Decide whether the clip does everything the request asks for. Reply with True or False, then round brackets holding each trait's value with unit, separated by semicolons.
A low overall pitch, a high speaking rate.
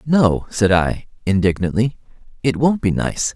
False (110 Hz; 145 wpm)